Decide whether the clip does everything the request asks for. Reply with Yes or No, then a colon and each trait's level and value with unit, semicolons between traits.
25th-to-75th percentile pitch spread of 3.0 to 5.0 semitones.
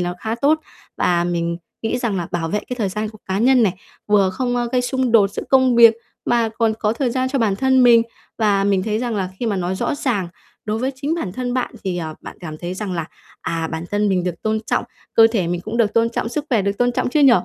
Yes: average, 4.6 semitones